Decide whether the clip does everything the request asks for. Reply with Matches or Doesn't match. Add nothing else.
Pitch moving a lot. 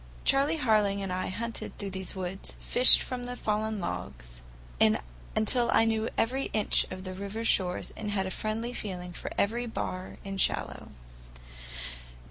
Doesn't match